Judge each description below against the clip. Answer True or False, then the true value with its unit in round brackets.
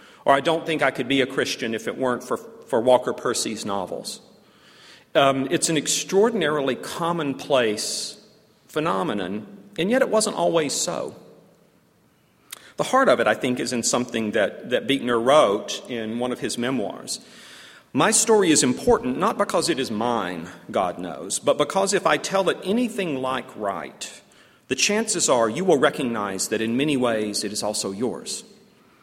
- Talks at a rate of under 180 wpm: True (165 wpm)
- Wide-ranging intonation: True (8.5 semitones)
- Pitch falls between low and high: True (150 Hz)